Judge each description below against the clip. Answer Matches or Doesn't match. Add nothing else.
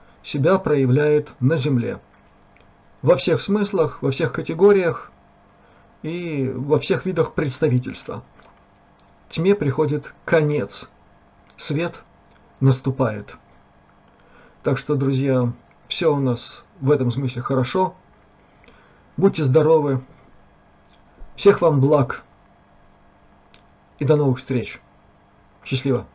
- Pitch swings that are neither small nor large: Matches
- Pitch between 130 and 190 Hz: Matches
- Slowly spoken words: Matches